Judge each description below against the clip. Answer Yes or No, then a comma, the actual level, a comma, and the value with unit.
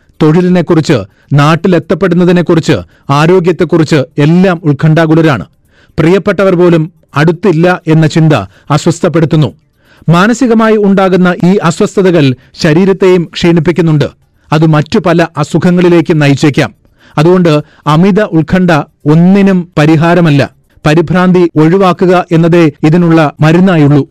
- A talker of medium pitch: Yes, medium, 170 Hz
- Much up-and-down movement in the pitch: No, average, 2.8 semitones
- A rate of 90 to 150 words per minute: No, average, 80 wpm